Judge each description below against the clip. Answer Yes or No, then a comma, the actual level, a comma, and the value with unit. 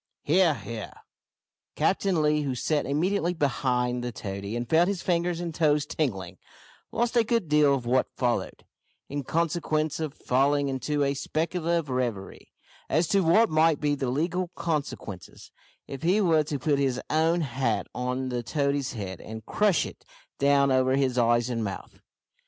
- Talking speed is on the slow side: No, average, 170 wpm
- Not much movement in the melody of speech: No, average, 4.7 semitones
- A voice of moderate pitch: Yes, medium, 145 Hz